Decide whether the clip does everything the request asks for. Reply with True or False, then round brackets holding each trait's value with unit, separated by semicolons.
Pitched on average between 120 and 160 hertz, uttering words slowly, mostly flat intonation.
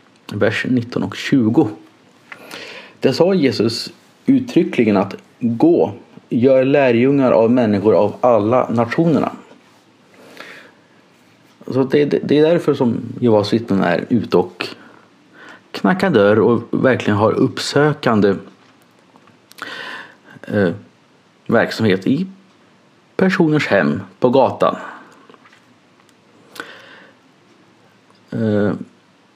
False (135 Hz; 90 wpm; 5.2 semitones)